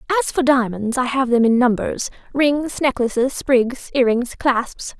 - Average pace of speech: Yes, average, 170 wpm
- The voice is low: No, very high, 255 Hz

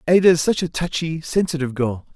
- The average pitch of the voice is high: No, medium, 155 Hz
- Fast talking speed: No, average, 195 wpm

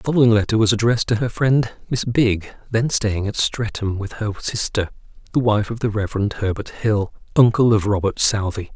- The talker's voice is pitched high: No, low, 110 Hz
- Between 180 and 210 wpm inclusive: Yes, average, 190 wpm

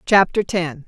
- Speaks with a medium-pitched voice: Yes, medium, 180 Hz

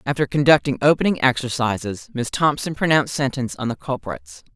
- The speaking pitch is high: No, low, 135 Hz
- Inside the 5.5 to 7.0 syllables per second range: Yes, 5.8 syllables/s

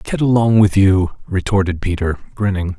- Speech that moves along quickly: No, average, 150 wpm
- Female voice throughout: No, male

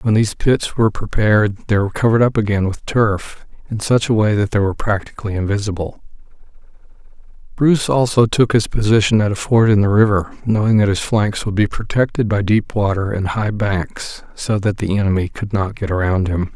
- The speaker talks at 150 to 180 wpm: No, average, 195 wpm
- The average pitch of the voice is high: No, low, 105 Hz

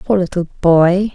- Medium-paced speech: Yes, average, 155 wpm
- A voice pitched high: No, medium, 180 Hz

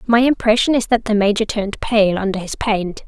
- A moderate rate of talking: No, fast, 215 wpm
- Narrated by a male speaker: No, female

